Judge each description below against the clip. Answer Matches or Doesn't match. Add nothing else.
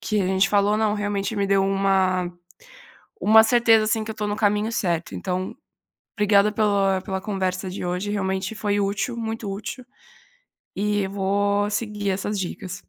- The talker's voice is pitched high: Matches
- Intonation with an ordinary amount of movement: Doesn't match